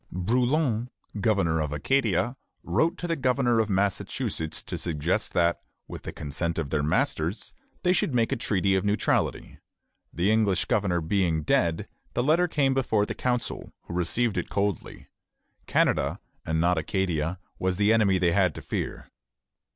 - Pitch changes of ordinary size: No, wide, 6.0 semitones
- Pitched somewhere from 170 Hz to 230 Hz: No, low, 100 Hz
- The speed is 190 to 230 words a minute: No, average, 160 wpm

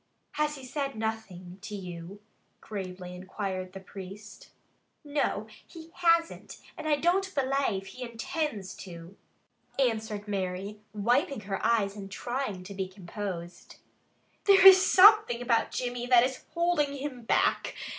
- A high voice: Yes, high, 220 Hz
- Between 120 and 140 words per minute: Yes, slow, 135 wpm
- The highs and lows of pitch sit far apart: Yes, wide, 6.4 semitones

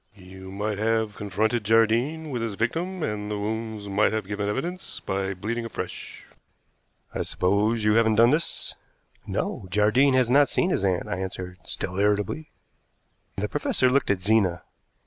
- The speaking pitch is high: No, low, 110 Hz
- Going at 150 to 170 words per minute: Yes, average, 160 wpm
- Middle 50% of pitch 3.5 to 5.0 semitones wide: No, average, 3.0 semitones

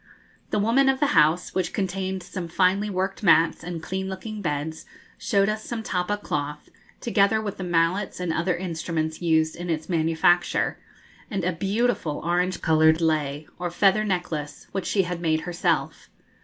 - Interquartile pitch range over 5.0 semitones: No, average, 3.3 semitones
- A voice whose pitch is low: No, medium, 180 Hz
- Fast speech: No, average, 165 wpm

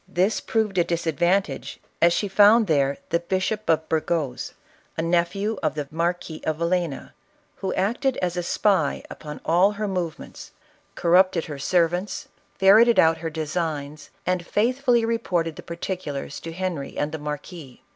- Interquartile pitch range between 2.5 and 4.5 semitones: Yes, average, 3.5 semitones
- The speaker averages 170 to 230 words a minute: Yes, average, 175 wpm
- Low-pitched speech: No, medium, 170 Hz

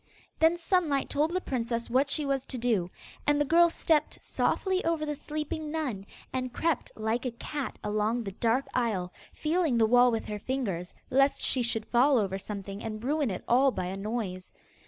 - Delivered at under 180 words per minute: No, average, 190 wpm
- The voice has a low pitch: No, very high, 250 Hz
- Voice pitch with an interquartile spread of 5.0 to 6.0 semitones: Yes, wide, 5.5 semitones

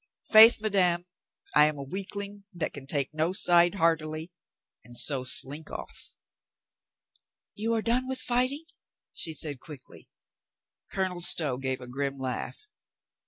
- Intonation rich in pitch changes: Yes, wide, 6.3 semitones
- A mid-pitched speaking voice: Yes, medium, 165 Hz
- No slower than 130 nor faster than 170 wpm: Yes, average, 140 wpm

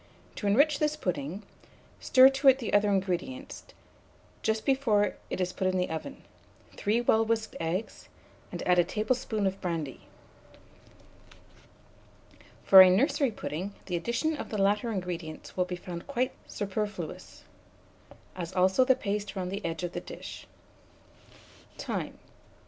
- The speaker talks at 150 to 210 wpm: No, average, 140 wpm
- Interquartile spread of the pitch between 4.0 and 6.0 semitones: Yes, average, 4.7 semitones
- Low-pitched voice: No, high, 200 Hz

